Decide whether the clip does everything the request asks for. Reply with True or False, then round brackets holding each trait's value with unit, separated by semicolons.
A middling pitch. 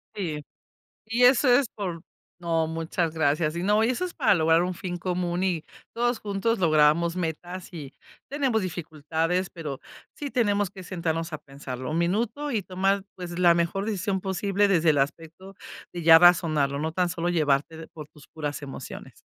True (175 Hz)